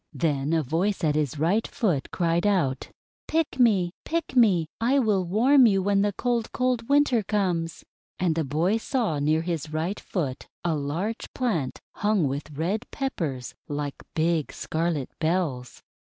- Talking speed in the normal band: Yes, average, 155 wpm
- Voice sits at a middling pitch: Yes, medium, 175 Hz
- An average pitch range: No, wide, 6.0 semitones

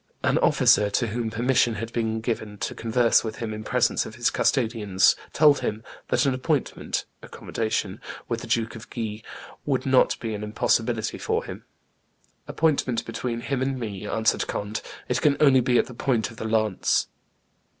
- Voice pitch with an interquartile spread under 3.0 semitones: Yes, narrow, 2.6 semitones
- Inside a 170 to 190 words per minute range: Yes, average, 175 wpm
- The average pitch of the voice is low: Yes, low, 115 Hz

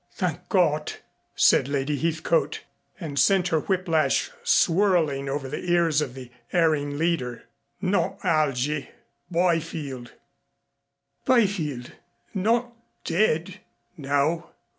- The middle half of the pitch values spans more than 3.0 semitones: Yes, average, 4.3 semitones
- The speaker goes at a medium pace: No, slow, 105 wpm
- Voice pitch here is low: No, medium, 160 Hz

